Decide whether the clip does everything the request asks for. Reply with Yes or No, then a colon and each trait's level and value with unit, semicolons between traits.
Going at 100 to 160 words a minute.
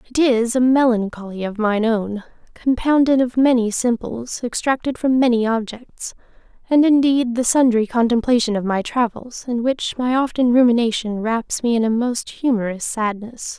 Yes: average, 155 wpm